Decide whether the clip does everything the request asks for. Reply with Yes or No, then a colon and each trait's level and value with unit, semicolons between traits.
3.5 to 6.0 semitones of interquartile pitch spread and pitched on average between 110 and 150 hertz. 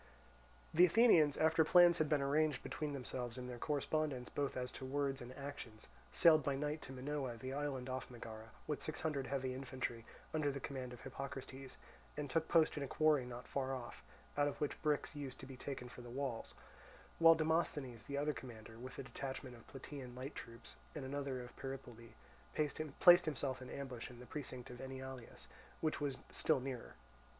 No: average, 2.8 semitones; low, 135 Hz